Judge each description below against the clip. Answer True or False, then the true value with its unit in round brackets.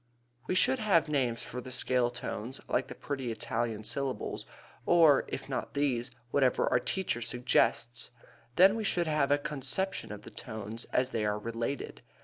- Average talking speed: True (165 wpm)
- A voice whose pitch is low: True (130 Hz)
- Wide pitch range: False (4.3 semitones)